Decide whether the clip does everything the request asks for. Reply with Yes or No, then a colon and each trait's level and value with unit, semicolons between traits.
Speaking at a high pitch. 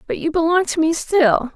Yes: very high, 320 Hz